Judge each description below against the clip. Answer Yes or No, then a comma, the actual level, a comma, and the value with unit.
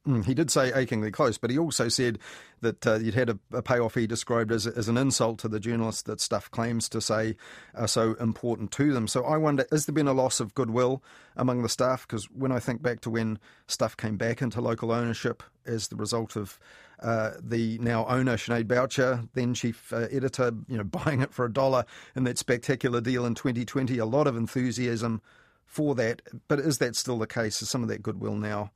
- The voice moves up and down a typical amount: No, narrow, 2.2 semitones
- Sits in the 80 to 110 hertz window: No, low, 120 Hz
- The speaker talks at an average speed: No, fast, 225 wpm